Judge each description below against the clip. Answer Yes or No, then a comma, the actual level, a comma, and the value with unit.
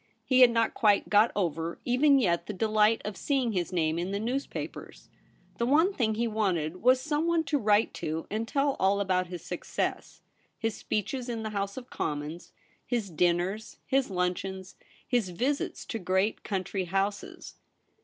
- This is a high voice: Yes, high, 210 Hz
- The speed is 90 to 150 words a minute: No, average, 165 wpm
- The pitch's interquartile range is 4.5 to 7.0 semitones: Yes, average, 4.9 semitones